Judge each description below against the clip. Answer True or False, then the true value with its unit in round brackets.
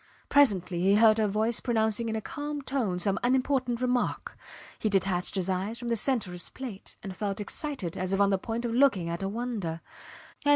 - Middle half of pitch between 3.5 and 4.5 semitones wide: True (4.2 semitones)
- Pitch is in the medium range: False (215 Hz)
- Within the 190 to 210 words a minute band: True (205 wpm)